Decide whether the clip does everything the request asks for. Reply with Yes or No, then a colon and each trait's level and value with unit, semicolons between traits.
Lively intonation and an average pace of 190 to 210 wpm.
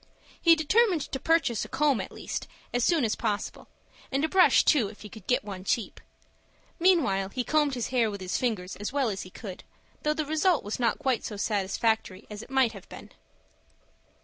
Yes: wide, 6.5 semitones; average, 200 wpm